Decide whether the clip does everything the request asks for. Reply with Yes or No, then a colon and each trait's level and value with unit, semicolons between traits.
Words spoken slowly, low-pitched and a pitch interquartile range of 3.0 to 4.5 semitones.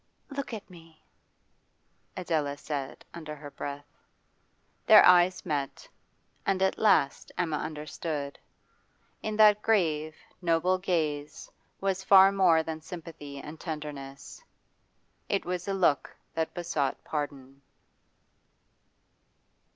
No: slow, 105 wpm; medium, 160 Hz; average, 4.0 semitones